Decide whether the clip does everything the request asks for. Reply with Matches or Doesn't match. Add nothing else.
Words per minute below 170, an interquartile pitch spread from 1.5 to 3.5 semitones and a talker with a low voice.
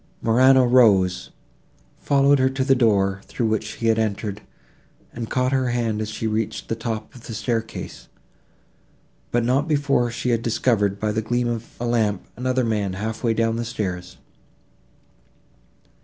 Matches